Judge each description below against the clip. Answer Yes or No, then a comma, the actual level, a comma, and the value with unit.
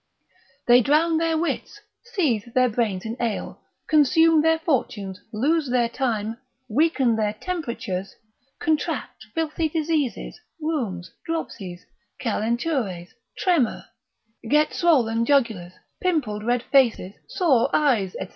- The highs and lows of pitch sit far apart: Yes, wide, 6.3 semitones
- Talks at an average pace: No, slow, 110 wpm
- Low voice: No, very high, 255 Hz